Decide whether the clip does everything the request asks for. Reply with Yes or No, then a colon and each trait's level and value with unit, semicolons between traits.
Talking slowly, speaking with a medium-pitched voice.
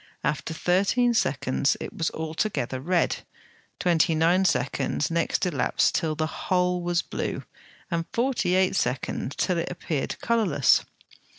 Yes: slow, 130 wpm; medium, 170 Hz